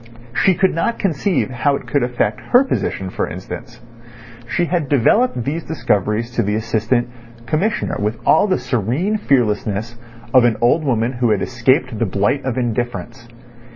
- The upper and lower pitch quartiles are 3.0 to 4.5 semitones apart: No, wide, 5.4 semitones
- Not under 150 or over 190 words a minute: Yes, average, 160 wpm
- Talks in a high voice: No, low, 125 Hz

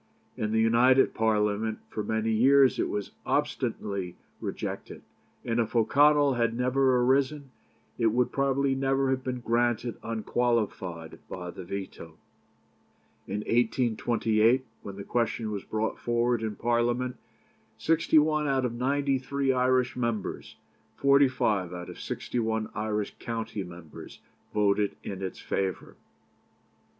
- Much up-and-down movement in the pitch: No, average, 3.5 semitones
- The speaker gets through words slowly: Yes, slow, 130 wpm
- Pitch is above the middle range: No, low, 115 Hz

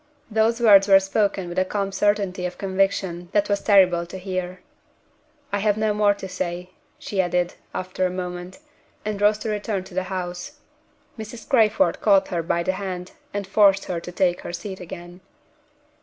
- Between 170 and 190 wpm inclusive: Yes, average, 180 wpm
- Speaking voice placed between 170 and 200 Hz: Yes, high, 190 Hz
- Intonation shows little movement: Yes, narrow, 2.3 semitones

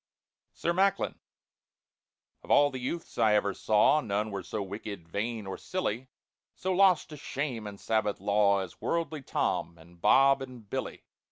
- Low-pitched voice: Yes, low, 110 Hz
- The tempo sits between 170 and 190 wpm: No, average, 160 wpm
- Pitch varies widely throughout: Yes, wide, 6.2 semitones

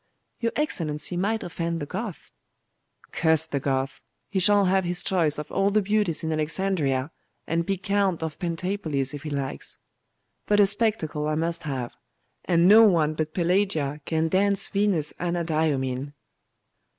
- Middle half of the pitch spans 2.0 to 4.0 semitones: No, average, 4.4 semitones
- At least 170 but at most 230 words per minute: No, average, 150 wpm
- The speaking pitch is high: No, medium, 170 Hz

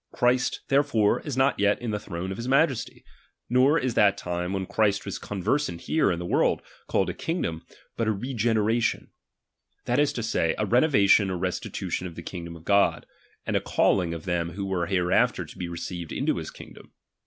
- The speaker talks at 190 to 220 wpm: Yes, average, 200 wpm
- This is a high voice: No, low, 100 Hz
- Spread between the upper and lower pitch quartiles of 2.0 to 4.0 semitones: No, wide, 5.6 semitones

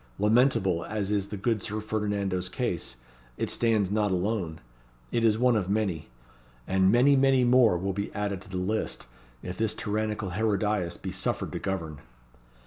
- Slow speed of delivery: No, average, 165 wpm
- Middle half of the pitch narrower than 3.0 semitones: Yes, narrow, 2.6 semitones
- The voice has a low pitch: Yes, low, 105 Hz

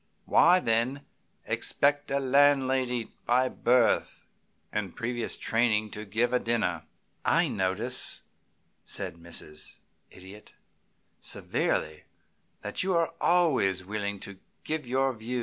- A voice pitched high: No, low, 120 Hz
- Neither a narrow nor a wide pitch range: Yes, average, 4.3 semitones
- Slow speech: Yes, slow, 115 wpm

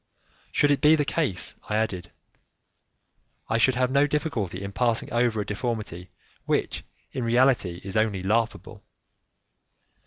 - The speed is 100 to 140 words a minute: Yes, slow, 135 wpm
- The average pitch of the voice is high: No, low, 115 Hz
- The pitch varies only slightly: No, average, 4.8 semitones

